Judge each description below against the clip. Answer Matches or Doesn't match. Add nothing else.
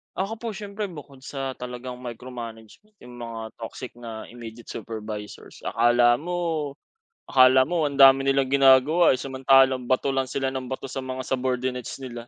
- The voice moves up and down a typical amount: Doesn't match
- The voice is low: Matches